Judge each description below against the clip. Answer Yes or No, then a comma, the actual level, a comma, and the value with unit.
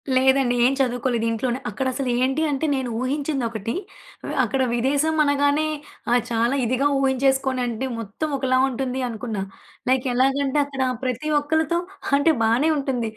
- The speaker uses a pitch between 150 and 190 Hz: No, very high, 265 Hz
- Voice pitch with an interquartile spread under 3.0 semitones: Yes, narrow, 2.4 semitones